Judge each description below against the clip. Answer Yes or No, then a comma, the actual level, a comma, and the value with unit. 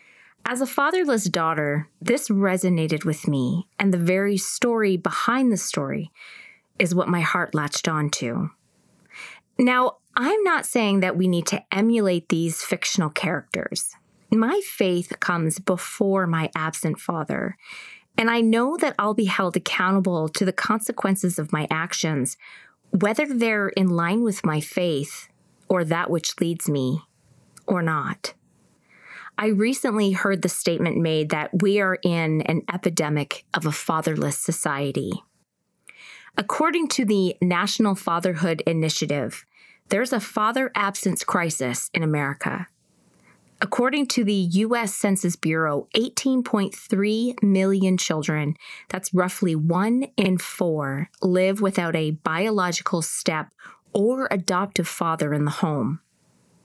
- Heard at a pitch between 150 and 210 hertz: Yes, medium, 185 Hz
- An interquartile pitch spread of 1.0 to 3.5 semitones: No, average, 4.7 semitones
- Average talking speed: No, slow, 130 wpm